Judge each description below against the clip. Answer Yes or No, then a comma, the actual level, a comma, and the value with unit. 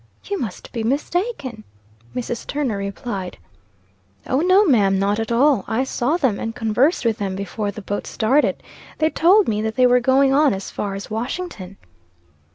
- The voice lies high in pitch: Yes, high, 235 Hz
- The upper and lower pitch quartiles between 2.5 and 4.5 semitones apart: No, wide, 5.4 semitones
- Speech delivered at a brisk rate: No, average, 170 wpm